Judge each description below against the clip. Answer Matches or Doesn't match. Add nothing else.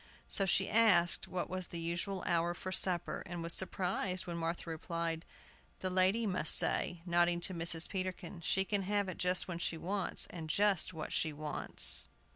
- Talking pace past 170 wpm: Matches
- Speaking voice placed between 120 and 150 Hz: Doesn't match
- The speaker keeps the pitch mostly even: Matches